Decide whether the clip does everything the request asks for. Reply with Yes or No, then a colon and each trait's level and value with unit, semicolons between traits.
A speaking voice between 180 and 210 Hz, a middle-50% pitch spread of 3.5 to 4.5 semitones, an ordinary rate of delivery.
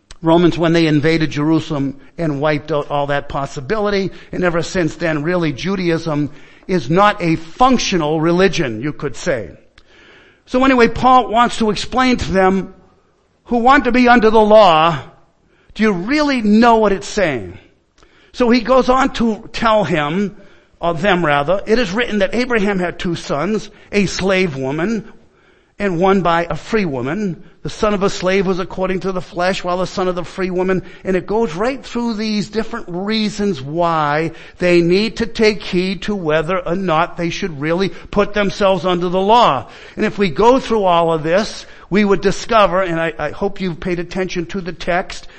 Yes: high, 190 Hz; average, 4.2 semitones; average, 180 wpm